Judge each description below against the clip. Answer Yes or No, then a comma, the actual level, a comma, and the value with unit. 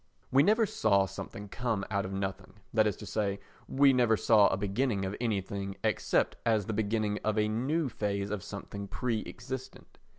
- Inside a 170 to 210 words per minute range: Yes, average, 185 wpm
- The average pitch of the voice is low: Yes, low, 105 Hz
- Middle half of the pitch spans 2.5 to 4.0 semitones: Yes, average, 2.9 semitones